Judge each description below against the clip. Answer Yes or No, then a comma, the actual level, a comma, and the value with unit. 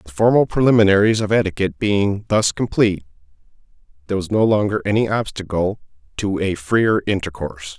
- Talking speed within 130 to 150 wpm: Yes, average, 140 wpm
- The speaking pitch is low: Yes, low, 100 Hz